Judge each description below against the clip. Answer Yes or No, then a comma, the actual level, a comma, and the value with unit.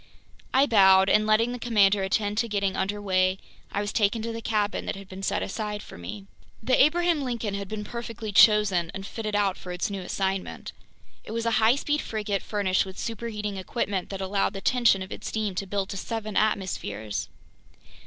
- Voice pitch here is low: No, high, 205 Hz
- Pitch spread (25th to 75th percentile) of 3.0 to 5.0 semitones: No, narrow, 2.6 semitones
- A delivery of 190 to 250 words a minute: Yes, average, 200 wpm